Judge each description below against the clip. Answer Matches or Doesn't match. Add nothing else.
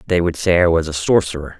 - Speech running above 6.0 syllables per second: Matches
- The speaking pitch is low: Matches